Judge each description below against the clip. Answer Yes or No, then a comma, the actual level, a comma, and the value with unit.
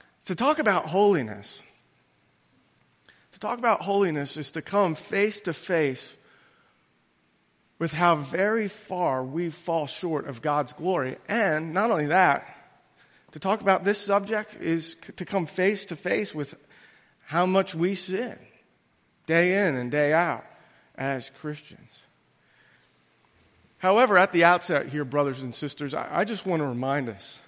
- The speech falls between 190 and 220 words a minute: No, average, 140 wpm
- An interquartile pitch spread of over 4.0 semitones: Yes, average, 5.1 semitones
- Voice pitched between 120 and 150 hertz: No, medium, 170 Hz